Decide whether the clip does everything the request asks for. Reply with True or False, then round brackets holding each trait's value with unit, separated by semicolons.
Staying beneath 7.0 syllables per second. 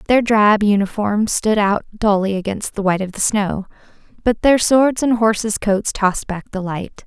True (4.5 syllables/s)